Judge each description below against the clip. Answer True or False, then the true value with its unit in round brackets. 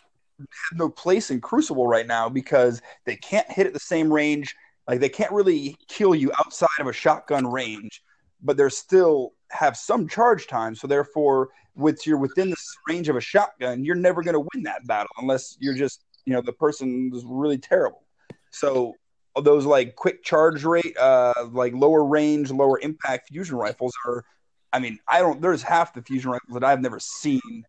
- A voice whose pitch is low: False (150 Hz)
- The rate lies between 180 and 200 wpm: True (190 wpm)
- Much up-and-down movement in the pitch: True (6.1 semitones)